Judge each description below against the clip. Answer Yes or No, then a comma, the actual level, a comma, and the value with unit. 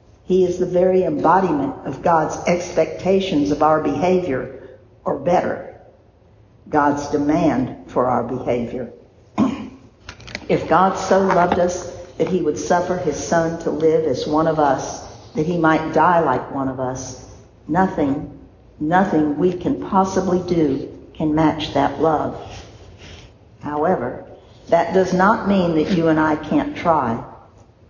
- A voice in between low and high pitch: Yes, medium, 155 Hz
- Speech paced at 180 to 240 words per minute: No, average, 140 wpm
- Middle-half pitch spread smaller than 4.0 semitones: No, average, 4.8 semitones